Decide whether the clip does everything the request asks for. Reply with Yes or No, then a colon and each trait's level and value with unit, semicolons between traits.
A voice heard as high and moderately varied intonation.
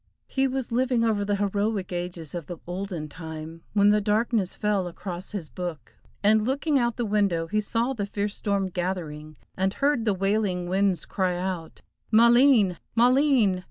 Yes: high, 200 Hz; average, 4.1 semitones